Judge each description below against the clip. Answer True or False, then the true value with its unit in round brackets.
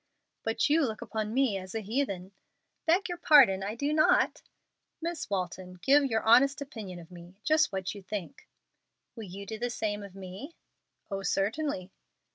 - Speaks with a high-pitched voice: True (215 Hz)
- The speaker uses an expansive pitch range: True (6.4 semitones)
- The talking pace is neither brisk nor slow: True (170 wpm)